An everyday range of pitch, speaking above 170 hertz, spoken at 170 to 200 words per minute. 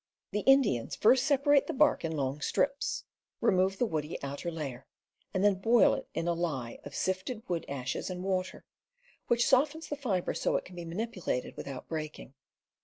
No: wide, 7.6 semitones; medium, 185 Hz; average, 180 wpm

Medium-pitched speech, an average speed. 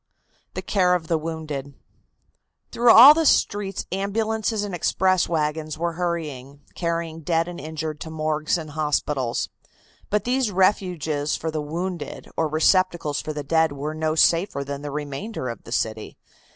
Yes: medium, 160 Hz; average, 155 wpm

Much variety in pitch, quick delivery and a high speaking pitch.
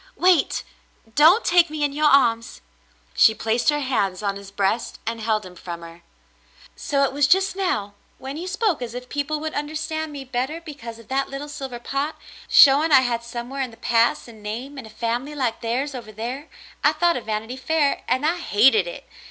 No: average, 4.6 semitones; fast, 210 wpm; very high, 265 Hz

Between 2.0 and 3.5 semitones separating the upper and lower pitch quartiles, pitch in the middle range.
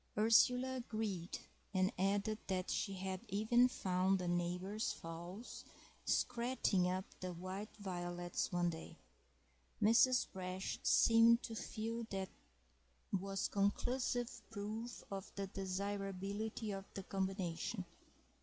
No: average, 3.2 semitones; high, 195 Hz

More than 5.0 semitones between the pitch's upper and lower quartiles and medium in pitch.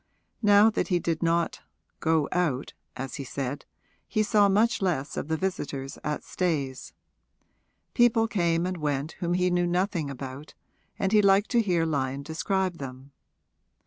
Yes: wide, 5.4 semitones; medium, 170 Hz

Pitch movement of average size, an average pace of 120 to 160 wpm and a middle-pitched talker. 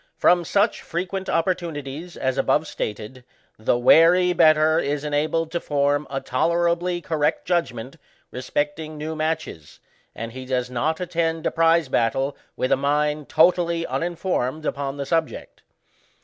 Yes: average, 3.6 semitones; average, 140 wpm; medium, 155 Hz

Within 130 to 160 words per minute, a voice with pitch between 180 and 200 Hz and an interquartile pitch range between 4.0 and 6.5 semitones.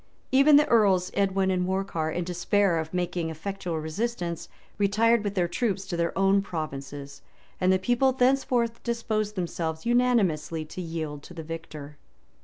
Yes: average, 155 wpm; medium, 185 Hz; average, 4.9 semitones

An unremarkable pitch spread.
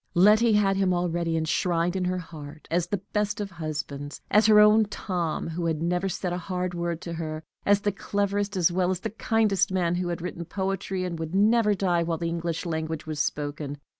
Yes: average, 3.0 semitones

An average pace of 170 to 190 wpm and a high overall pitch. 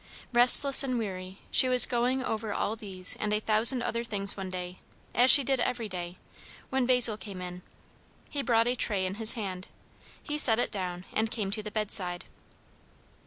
Yes: average, 185 wpm; high, 215 Hz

